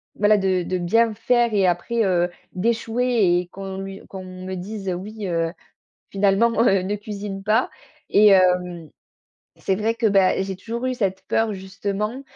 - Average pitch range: Yes, average, 3.0 semitones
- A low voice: No, high, 195 Hz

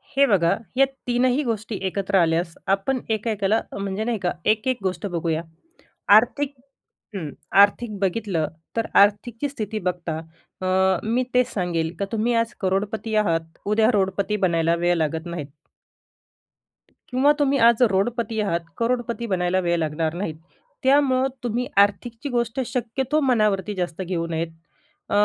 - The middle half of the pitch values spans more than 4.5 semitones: Yes, average, 5.0 semitones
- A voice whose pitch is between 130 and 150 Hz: No, high, 205 Hz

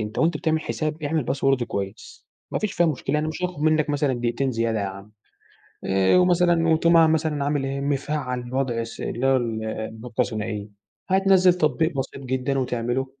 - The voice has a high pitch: No, low, 135 Hz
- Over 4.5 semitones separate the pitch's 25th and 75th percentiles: Yes, average, 5.0 semitones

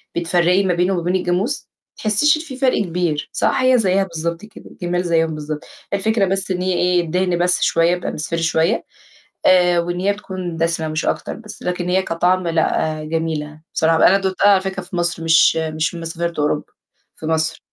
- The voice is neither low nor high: Yes, medium, 175 Hz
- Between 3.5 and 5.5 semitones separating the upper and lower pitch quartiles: No, narrow, 2.5 semitones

